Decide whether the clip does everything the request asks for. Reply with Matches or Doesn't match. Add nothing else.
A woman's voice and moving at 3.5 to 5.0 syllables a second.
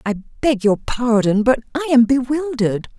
Matches